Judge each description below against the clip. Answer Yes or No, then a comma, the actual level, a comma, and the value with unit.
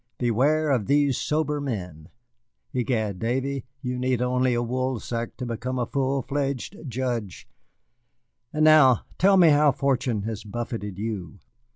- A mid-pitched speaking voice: No, low, 125 Hz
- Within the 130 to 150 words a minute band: Yes, average, 140 wpm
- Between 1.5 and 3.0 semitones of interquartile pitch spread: No, average, 3.4 semitones